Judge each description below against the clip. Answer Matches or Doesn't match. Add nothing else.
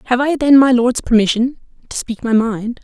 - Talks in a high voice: Matches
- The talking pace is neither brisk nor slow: Doesn't match